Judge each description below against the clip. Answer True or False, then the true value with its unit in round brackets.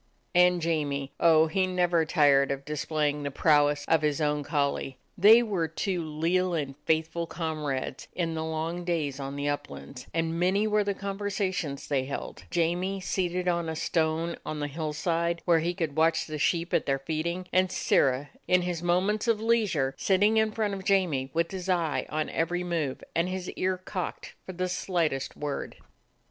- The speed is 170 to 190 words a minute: True (185 wpm)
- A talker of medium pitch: True (165 Hz)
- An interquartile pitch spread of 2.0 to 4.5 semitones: True (3.5 semitones)